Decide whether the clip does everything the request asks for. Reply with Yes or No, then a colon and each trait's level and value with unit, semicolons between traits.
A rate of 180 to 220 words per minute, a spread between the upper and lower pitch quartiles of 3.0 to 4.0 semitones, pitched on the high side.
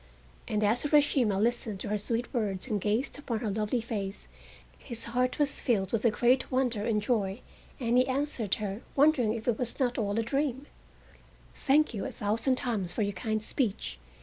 Yes: average, 190 wpm; average, 3.3 semitones; high, 230 Hz